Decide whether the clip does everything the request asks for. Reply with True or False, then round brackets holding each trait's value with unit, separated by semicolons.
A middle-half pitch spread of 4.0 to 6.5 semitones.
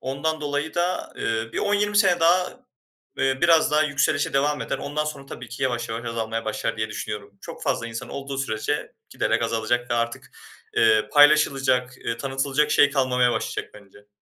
True (4.6 semitones)